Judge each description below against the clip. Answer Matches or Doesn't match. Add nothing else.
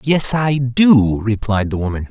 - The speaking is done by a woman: Doesn't match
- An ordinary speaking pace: Matches